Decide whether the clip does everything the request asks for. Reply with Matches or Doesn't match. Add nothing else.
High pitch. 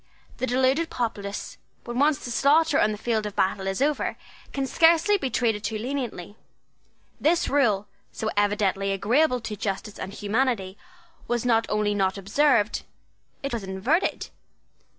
Matches